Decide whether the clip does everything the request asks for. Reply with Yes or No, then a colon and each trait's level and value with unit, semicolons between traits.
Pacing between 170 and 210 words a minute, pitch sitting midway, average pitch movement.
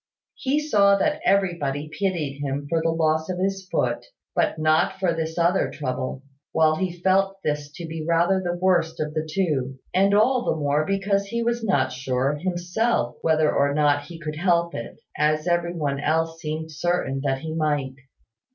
Yes: average, 180 wpm; medium, 160 Hz; average, 4.0 semitones